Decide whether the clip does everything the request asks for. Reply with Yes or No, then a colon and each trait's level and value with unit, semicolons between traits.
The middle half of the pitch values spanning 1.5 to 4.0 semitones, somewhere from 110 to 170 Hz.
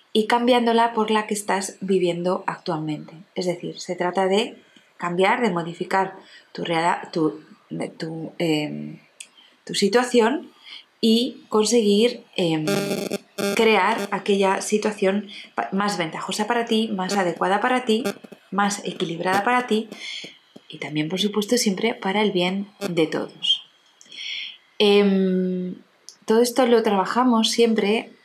No: average, 3.4 semitones; high, 200 Hz